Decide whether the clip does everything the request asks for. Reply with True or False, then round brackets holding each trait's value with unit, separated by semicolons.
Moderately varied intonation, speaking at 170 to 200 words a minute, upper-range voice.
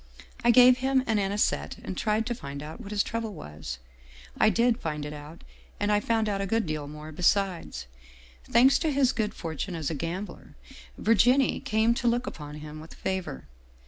False (7.1 semitones; 195 wpm; 200 Hz)